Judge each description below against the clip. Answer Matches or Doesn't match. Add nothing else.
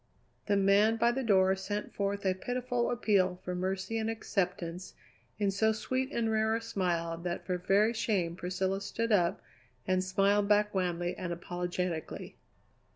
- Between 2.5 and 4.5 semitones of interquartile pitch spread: Matches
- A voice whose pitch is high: Matches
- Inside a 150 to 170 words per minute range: Matches